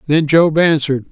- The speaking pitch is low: No, medium, 150 Hz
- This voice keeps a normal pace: Yes, average, 160 wpm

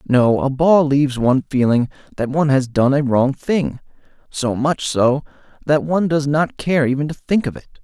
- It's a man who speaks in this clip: Yes, male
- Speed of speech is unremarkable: Yes, average, 190 wpm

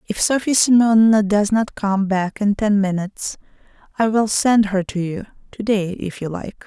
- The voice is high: Yes, high, 205 Hz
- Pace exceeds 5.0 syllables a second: No, 4.8 syllables/s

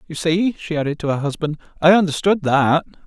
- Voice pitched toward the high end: No, medium, 160 Hz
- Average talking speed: Yes, average, 195 wpm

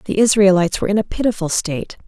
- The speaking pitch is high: Yes, high, 195 Hz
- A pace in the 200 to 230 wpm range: Yes, fast, 205 wpm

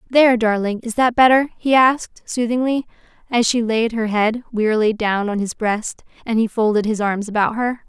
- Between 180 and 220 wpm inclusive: Yes, average, 190 wpm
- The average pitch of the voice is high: Yes, high, 225 Hz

